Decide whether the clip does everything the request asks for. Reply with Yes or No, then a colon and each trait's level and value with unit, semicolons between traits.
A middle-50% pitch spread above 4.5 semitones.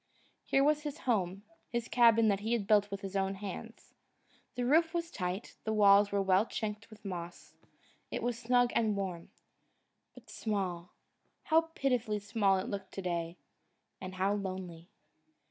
No: average, 3.6 semitones